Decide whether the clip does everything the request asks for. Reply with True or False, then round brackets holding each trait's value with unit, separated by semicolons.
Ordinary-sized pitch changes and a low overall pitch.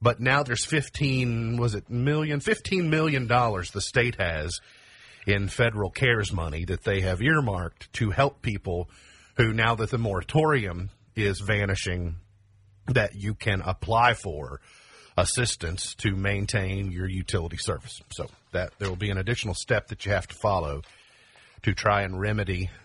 True (4.2 semitones; 105 Hz)